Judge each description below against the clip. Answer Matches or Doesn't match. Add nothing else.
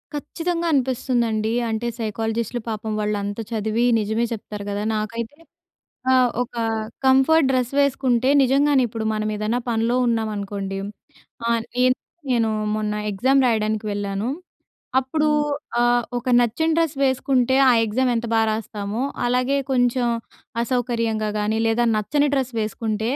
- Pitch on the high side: Matches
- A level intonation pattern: Doesn't match